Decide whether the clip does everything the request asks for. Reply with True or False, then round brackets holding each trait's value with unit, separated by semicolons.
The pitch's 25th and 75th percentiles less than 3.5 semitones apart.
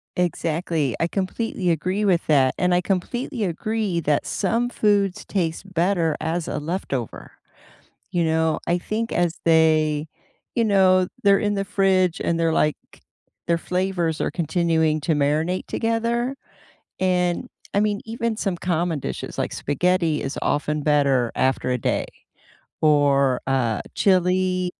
False (3.9 semitones)